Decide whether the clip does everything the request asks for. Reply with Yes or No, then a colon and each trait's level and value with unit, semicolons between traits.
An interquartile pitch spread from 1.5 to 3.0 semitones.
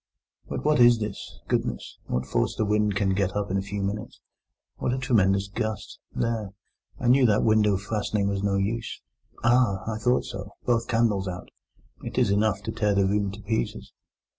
Yes: narrow, 2.6 semitones